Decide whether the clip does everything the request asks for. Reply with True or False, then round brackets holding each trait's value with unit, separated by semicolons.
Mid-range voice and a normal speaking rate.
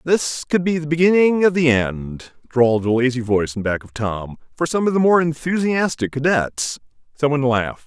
True (145 Hz; 190 wpm)